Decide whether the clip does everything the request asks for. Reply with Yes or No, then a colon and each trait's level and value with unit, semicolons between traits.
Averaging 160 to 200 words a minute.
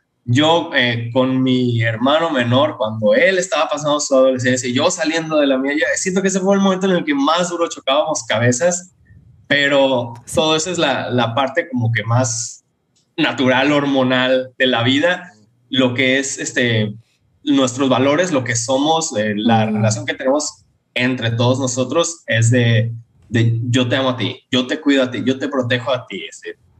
Yes: average, 180 wpm